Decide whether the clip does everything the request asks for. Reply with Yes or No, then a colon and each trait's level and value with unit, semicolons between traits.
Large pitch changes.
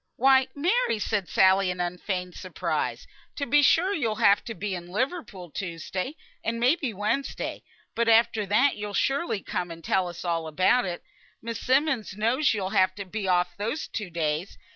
Yes: wide, 5.7 semitones